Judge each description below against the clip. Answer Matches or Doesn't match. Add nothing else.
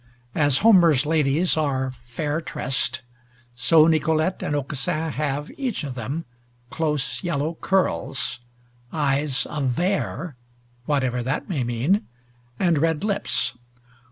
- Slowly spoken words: Matches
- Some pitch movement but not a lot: Matches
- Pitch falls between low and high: Matches